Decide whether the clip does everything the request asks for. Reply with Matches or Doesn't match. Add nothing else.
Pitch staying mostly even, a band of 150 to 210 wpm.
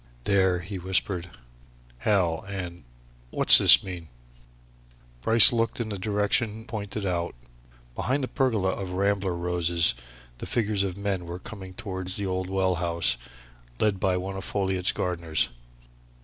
Doesn't match